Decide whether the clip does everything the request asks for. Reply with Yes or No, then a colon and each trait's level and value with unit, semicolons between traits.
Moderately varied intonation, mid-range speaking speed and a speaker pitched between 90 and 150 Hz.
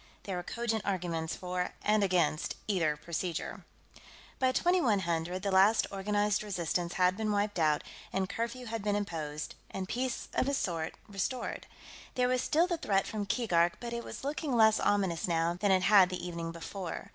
No: average, 4.1 semitones; average, 175 wpm; high, 195 Hz